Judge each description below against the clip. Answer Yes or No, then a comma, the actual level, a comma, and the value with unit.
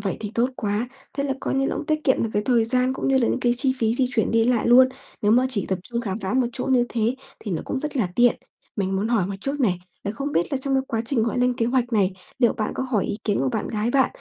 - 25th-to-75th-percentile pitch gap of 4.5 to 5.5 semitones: No, average, 3.6 semitones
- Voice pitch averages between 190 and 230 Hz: No, high, 240 Hz